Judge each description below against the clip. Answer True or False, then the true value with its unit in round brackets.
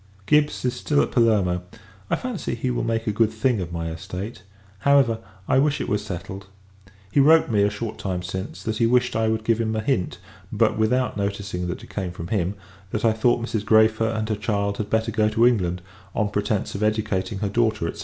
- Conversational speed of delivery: False (220 wpm)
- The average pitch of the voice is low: True (110 Hz)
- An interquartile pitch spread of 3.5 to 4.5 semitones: False (2.6 semitones)